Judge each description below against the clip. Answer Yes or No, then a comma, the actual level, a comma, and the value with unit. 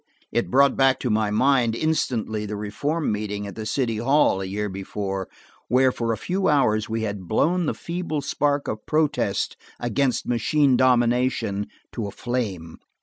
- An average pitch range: Yes, average, 4.8 semitones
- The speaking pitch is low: Yes, low, 120 Hz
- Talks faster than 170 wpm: No, average, 165 wpm